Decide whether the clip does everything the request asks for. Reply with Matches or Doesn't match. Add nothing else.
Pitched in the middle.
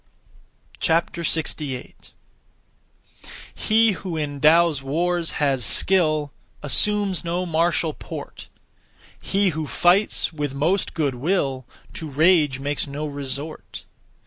Matches